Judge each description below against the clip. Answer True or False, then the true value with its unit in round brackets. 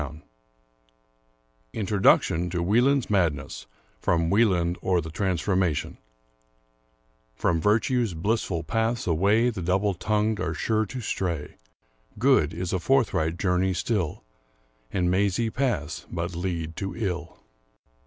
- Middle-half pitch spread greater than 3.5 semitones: True (4.7 semitones)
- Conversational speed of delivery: False (125 wpm)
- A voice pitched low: True (90 Hz)